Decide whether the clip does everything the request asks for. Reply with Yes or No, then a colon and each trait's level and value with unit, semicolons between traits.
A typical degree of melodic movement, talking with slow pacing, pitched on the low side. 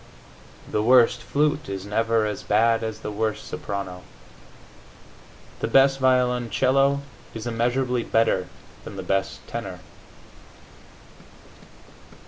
Yes: average, 3.4 semitones; slow, 105 wpm; low, 115 Hz